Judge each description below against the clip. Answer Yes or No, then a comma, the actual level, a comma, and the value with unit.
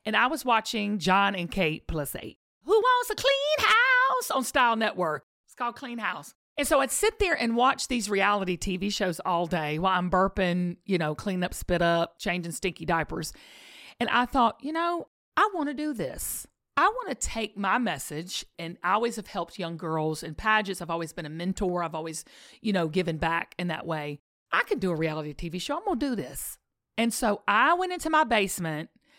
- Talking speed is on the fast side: Yes, fast, 210 wpm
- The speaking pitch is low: No, high, 200 Hz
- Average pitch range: No, wide, 7.5 semitones